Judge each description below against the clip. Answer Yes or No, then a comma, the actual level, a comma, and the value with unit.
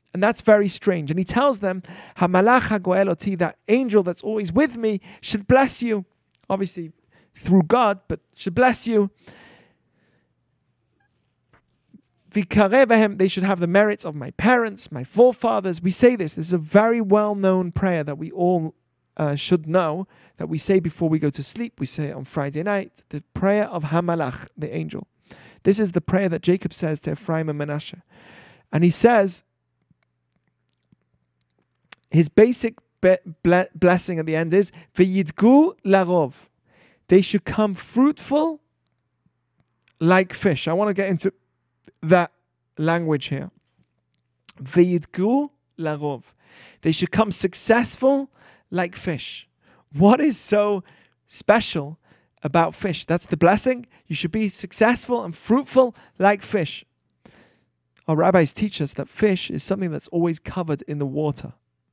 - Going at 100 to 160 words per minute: Yes, average, 140 wpm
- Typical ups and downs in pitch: Yes, average, 4.8 semitones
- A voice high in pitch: No, medium, 180 Hz